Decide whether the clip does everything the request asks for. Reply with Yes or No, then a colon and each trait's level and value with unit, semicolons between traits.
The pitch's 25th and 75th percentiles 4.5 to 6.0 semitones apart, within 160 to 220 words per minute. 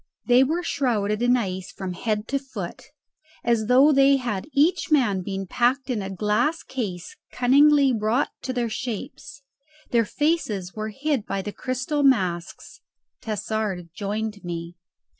No: average, 5.0 semitones; average, 145 wpm